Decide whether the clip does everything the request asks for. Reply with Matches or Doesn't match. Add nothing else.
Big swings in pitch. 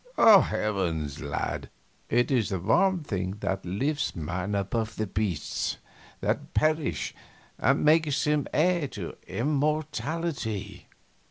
Matches